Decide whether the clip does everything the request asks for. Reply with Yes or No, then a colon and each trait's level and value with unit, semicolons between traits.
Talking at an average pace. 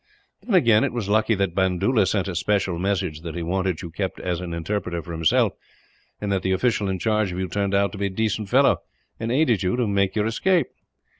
No: fast, 220 wpm